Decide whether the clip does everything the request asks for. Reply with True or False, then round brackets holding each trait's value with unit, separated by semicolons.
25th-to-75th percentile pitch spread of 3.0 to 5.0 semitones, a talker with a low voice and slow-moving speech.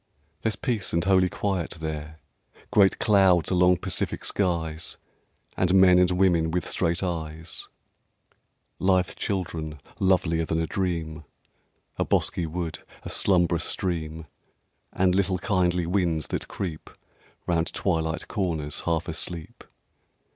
False (2.4 semitones; 90 Hz; 120 wpm)